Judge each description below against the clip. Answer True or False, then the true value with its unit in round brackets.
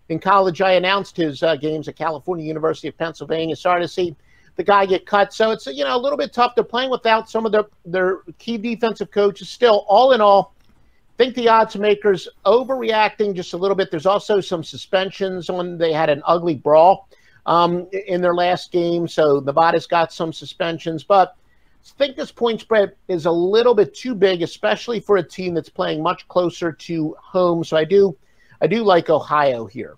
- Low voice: False (185 Hz)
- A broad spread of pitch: False (4.0 semitones)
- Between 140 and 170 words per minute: False (200 wpm)